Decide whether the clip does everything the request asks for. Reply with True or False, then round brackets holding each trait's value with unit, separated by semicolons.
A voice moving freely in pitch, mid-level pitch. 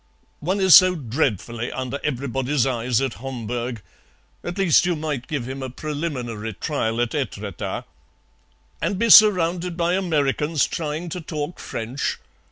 True (5.7 semitones; 145 Hz)